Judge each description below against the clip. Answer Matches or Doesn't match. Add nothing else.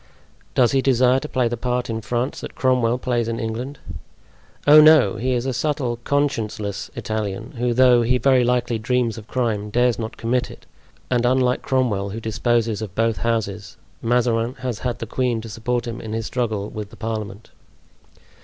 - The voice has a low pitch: Matches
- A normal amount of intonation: Doesn't match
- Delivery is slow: Doesn't match